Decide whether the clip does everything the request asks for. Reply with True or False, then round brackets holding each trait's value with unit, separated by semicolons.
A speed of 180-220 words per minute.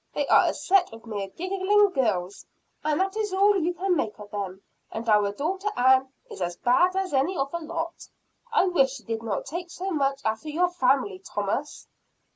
True (200 wpm)